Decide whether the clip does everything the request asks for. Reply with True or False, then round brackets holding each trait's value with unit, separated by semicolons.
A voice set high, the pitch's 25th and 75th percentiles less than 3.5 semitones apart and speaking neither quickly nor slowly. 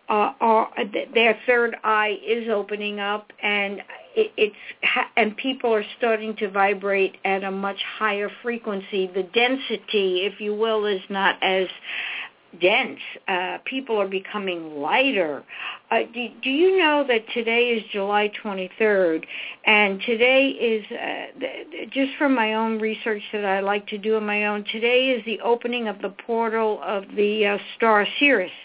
True (215 Hz; 2.7 semitones; 165 wpm)